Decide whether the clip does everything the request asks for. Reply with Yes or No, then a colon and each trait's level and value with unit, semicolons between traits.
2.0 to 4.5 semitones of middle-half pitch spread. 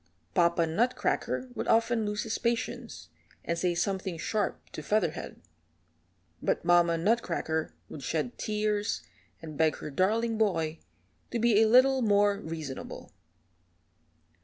No: average, 5.3 semitones